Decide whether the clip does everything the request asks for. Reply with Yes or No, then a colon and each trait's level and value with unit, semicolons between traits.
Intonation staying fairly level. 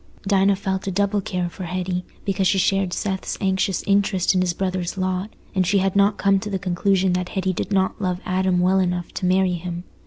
Yes: narrow, 1.2 semitones